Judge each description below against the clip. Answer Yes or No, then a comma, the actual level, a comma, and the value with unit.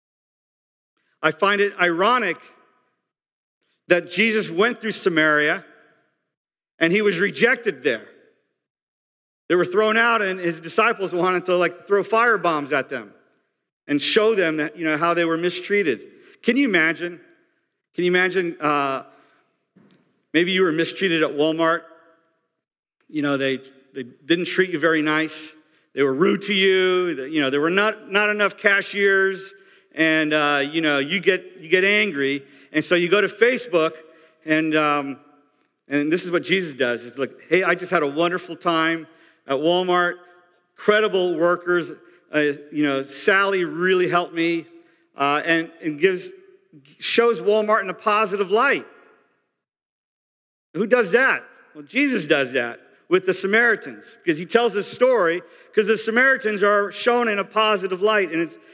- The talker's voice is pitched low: No, medium, 180 Hz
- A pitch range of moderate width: Yes, average, 4.6 semitones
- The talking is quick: No, average, 155 wpm